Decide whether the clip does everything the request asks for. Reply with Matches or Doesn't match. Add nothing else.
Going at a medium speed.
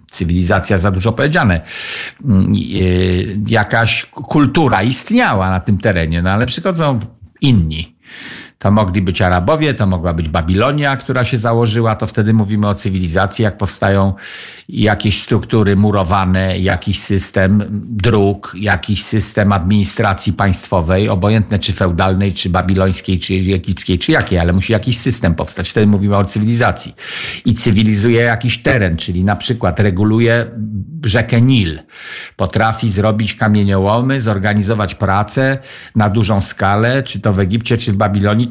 Matches